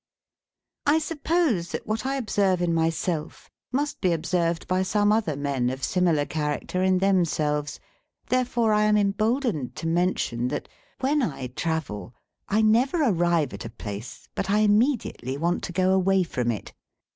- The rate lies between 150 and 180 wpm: Yes, average, 155 wpm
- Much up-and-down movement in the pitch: Yes, wide, 6.0 semitones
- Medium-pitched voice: Yes, medium, 180 Hz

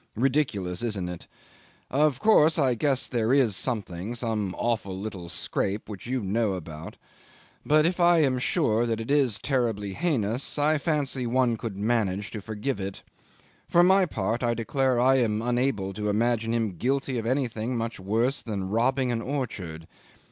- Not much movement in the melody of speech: No, average, 4.4 semitones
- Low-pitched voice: Yes, low, 115 Hz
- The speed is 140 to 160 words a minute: No, average, 170 wpm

